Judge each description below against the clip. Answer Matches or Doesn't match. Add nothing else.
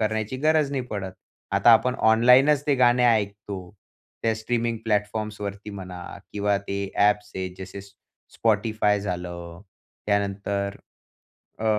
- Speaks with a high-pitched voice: Doesn't match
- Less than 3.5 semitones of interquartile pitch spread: Matches